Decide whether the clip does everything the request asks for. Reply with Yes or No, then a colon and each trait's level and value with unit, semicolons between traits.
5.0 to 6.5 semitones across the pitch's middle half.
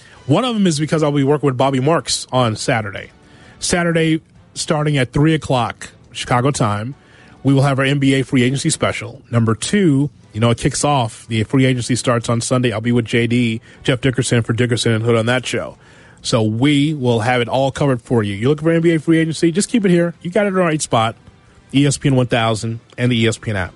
No: average, 3.9 semitones